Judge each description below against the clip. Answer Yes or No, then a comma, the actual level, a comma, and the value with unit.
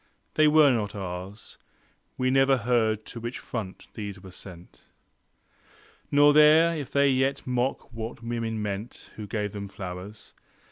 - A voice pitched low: Yes, low, 115 Hz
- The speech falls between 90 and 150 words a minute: Yes, average, 145 wpm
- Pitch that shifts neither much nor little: Yes, average, 4.8 semitones